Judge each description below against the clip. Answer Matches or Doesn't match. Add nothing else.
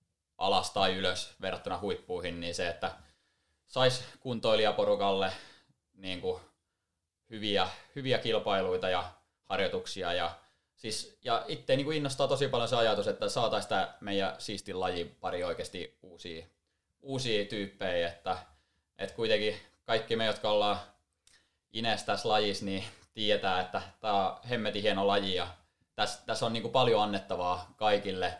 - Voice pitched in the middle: Doesn't match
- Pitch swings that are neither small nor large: Matches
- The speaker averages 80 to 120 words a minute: Doesn't match